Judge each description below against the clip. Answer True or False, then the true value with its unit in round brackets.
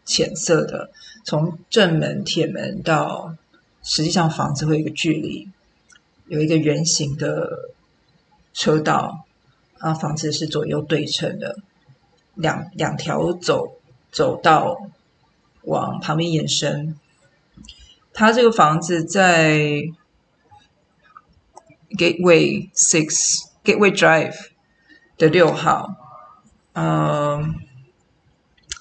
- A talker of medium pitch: True (160 Hz)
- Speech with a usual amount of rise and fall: True (3.5 semitones)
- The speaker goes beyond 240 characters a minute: False (170 characters per minute)